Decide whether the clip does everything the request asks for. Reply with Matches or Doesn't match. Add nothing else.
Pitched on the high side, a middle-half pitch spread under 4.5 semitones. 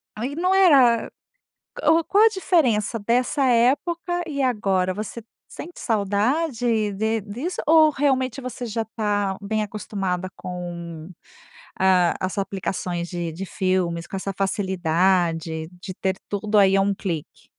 Doesn't match